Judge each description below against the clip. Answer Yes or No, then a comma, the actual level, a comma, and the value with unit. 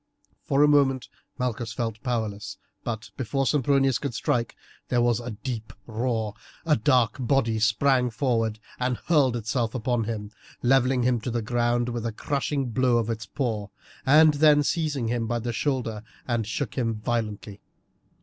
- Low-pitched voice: Yes, low, 120 Hz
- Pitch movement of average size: Yes, average, 3.0 semitones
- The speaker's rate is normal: Yes, average, 160 wpm